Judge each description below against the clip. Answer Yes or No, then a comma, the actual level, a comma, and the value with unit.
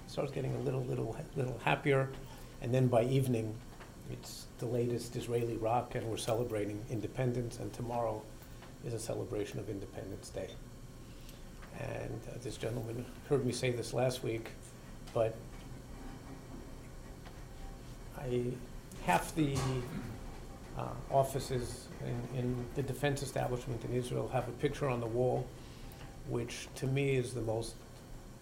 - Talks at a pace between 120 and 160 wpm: Yes, slow, 135 wpm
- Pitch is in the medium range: No, low, 125 Hz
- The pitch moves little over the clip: Yes, narrow, 2.1 semitones